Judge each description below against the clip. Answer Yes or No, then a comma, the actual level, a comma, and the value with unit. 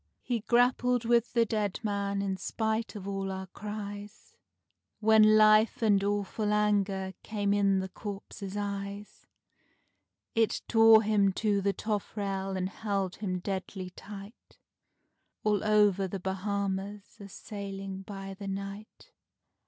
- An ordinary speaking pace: No, slow, 130 wpm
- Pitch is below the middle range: No, high, 200 Hz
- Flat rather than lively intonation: Yes, narrow, 1.6 semitones